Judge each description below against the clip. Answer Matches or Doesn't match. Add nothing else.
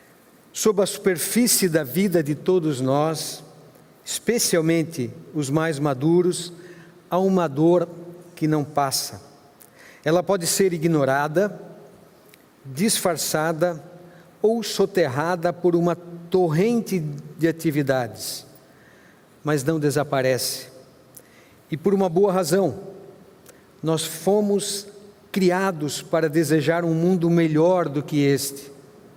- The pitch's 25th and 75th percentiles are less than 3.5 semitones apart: Doesn't match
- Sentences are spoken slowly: Matches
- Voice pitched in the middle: Matches